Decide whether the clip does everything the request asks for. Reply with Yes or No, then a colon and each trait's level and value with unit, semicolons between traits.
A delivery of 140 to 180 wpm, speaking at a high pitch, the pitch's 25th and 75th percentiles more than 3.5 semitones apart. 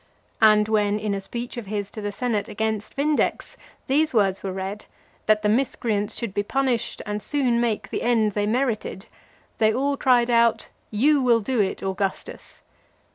No: average, 175 wpm; high, 220 Hz; average, 2.9 semitones